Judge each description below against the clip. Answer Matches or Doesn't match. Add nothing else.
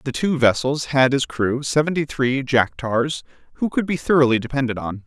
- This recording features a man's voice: Matches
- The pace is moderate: Matches